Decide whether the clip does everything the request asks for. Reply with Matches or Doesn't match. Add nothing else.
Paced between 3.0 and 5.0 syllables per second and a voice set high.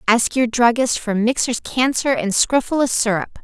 Matches